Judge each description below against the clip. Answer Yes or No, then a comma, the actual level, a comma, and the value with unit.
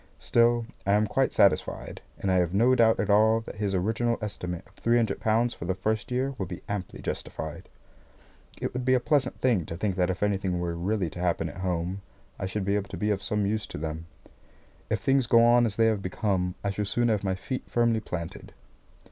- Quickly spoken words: Yes, fast, 225 wpm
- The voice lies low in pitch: Yes, low, 105 Hz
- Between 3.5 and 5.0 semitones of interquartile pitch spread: Yes, average, 3.8 semitones